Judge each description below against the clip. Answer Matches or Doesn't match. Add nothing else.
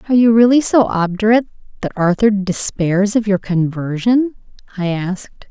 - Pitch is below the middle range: Doesn't match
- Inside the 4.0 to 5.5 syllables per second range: Matches